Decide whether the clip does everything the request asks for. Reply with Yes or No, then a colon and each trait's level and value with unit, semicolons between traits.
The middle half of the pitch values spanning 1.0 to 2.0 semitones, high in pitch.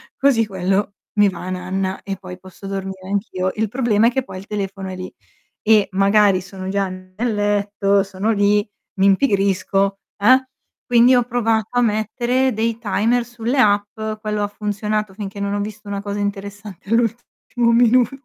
No: narrow, 2.5 semitones; high, 205 Hz